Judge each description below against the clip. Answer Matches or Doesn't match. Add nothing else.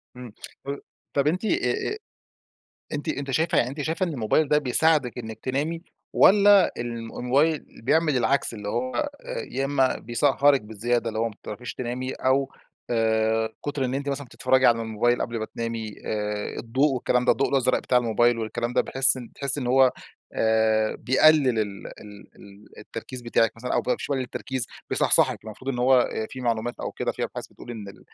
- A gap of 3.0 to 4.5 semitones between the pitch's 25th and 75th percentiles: Matches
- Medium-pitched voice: Doesn't match